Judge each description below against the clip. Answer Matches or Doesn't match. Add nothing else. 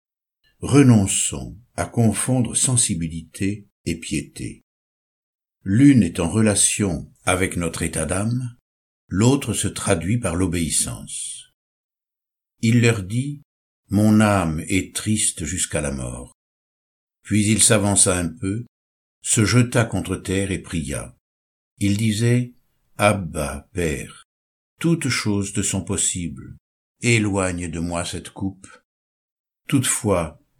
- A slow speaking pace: Matches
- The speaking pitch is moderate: Doesn't match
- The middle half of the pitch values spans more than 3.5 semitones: Matches